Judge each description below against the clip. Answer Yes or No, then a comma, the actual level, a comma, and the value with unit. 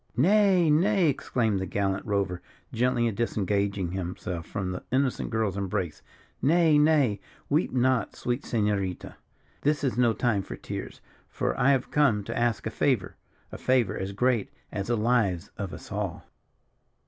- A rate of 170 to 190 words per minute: No, average, 155 wpm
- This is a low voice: Yes, low, 115 Hz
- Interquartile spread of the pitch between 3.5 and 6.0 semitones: Yes, average, 5.2 semitones